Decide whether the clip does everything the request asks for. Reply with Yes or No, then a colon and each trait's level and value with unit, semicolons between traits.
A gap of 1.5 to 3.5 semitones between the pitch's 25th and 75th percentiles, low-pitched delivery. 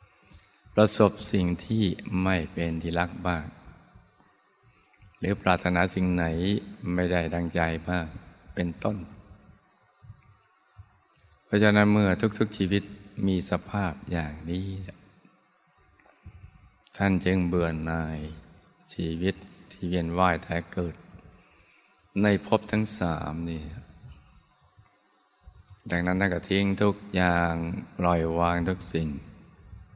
Yes: average, 2.8 semitones; very low, 90 Hz